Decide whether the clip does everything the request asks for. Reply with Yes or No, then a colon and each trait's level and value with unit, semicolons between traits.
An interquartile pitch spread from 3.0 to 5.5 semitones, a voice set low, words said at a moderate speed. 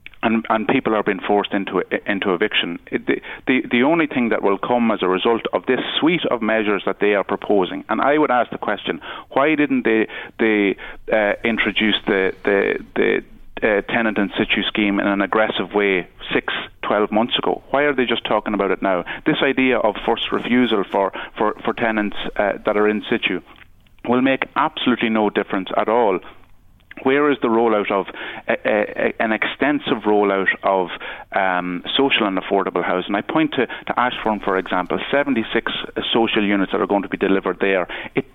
Yes: average, 3.3 semitones; low, 110 Hz; average, 190 wpm